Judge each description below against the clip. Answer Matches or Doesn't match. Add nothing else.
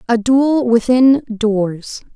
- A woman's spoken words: Matches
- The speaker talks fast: Doesn't match